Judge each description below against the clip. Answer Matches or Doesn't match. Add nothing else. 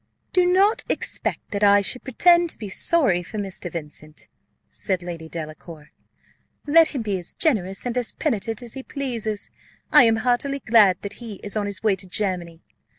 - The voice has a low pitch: Doesn't match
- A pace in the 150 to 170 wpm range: Doesn't match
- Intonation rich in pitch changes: Matches